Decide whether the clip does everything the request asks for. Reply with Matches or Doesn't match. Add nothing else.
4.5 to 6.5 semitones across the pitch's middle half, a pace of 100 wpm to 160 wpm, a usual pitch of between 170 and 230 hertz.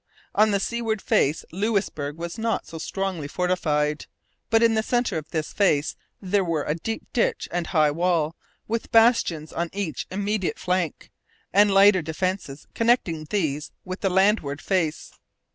Matches